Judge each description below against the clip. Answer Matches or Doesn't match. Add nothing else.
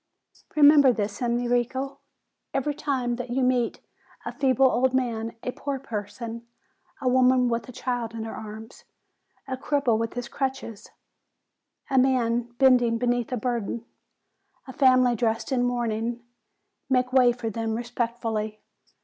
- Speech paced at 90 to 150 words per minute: Matches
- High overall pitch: Matches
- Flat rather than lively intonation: Matches